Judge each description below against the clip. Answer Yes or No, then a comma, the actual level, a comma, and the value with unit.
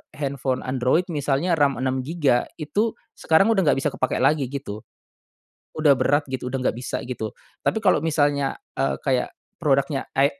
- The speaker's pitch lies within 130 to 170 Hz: Yes, medium, 140 Hz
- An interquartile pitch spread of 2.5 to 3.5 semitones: Yes, average, 2.8 semitones